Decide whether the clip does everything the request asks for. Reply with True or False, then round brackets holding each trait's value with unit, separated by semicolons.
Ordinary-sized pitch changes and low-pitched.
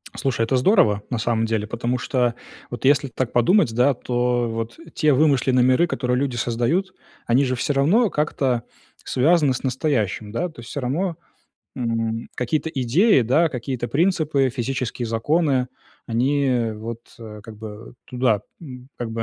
True (3.5 semitones; 125 Hz)